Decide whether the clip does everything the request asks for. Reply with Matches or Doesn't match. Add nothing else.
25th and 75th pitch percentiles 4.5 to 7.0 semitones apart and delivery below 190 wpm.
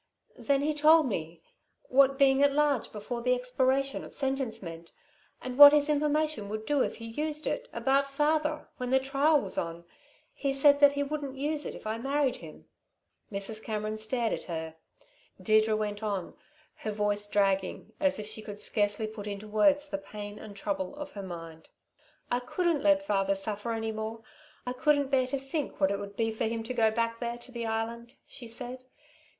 Doesn't match